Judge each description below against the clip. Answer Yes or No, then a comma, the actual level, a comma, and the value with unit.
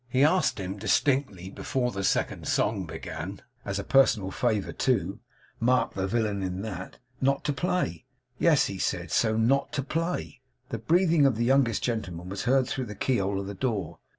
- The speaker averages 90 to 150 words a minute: No, average, 185 wpm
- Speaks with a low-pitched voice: Yes, low, 115 Hz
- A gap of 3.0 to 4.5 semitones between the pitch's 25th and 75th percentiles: No, wide, 5.5 semitones